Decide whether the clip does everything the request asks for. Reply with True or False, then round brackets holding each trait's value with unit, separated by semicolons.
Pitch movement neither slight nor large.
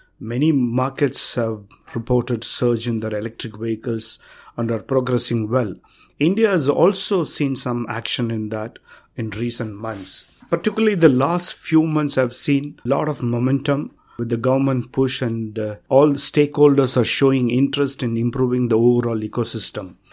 True (3.5 semitones)